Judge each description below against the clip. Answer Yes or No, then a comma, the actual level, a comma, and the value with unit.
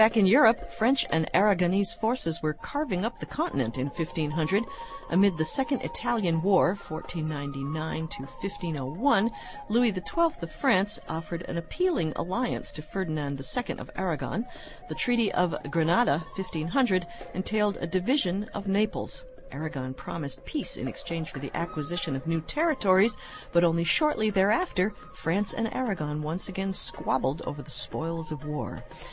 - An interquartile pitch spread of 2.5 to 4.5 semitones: No, average, 5.2 semitones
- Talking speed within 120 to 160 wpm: Yes, average, 140 wpm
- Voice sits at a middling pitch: Yes, medium, 180 Hz